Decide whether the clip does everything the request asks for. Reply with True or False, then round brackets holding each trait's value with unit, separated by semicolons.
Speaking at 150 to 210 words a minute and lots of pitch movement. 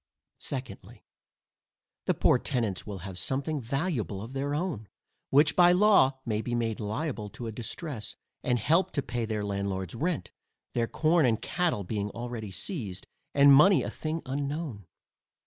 True (155 wpm; 5.9 semitones)